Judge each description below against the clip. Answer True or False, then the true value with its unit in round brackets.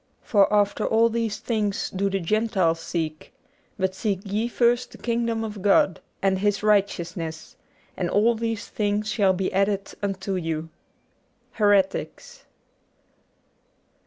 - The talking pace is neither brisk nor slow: False (130 wpm)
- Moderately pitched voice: False (205 Hz)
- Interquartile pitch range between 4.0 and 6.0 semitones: False (2.7 semitones)